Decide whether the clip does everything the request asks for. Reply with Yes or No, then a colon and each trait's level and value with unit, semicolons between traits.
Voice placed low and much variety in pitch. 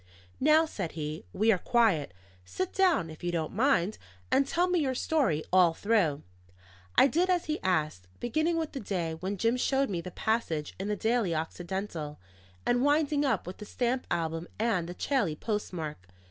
No: high, 205 Hz; wide, 8.4 semitones